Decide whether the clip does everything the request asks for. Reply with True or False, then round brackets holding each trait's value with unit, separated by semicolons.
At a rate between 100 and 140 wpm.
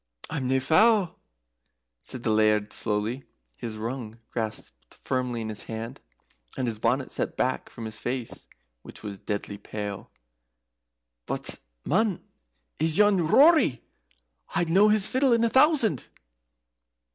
True (135 wpm)